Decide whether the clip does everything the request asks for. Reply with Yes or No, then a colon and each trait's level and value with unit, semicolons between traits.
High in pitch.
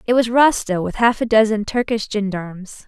Yes: high, 215 Hz